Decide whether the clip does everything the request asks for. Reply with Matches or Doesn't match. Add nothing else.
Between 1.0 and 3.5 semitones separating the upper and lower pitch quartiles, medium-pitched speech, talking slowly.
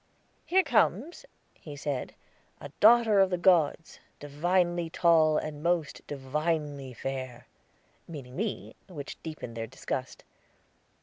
Doesn't match